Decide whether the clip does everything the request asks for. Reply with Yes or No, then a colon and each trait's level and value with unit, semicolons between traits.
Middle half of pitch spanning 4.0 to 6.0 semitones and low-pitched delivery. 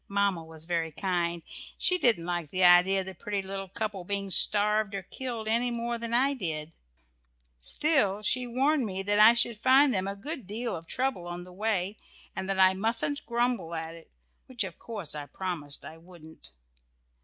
No: average, 4.9 semitones; high, 195 Hz